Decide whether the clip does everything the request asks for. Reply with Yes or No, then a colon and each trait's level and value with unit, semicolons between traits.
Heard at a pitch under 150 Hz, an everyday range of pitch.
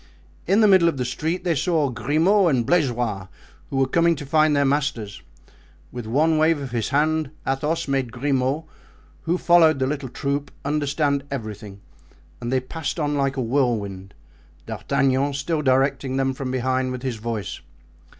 Yes: low, 135 Hz; average, 3.4 semitones